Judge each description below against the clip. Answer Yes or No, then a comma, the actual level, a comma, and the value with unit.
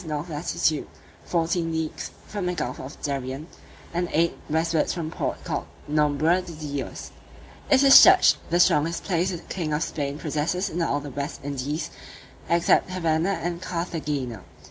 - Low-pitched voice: No, medium, 160 Hz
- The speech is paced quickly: No, average, 160 wpm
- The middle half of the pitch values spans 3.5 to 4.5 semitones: No, average, 3.0 semitones